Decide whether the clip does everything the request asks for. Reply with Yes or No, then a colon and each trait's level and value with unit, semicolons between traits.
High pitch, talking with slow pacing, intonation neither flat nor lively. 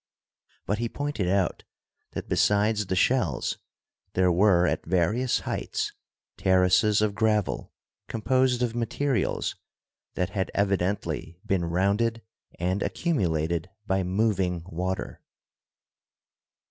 No: low, 100 Hz; slow, 105 wpm; average, 3.5 semitones